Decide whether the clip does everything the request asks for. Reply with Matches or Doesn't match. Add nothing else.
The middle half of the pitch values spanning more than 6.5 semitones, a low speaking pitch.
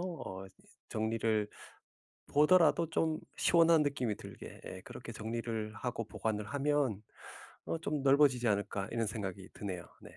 Doesn't match